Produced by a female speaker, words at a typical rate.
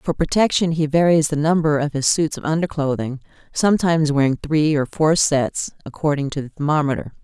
Yes: female; average, 175 wpm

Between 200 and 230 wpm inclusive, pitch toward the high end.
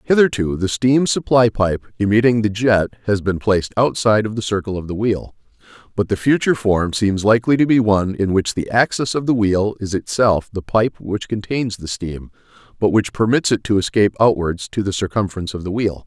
No: fast, 205 wpm; low, 105 Hz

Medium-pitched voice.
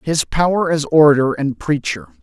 Yes: medium, 155 Hz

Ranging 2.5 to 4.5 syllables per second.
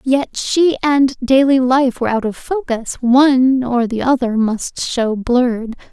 Yes: 4.0 syllables/s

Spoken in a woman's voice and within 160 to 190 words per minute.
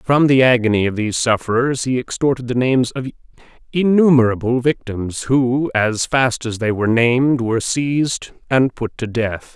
No: male; average, 165 wpm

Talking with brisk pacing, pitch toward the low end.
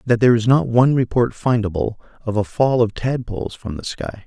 Yes: fast, 210 wpm; low, 115 Hz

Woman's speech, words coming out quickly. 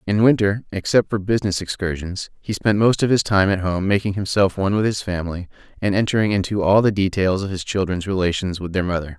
No: male; fast, 215 wpm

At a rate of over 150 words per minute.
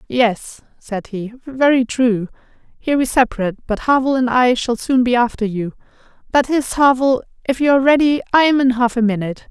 Yes: average, 190 wpm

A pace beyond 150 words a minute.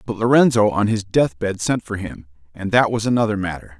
Yes: fast, 205 wpm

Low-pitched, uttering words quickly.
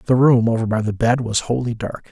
Yes: low, 115 Hz; fast, 255 wpm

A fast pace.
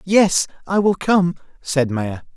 No: average, 155 wpm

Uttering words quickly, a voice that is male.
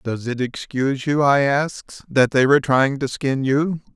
No: average, 195 wpm; male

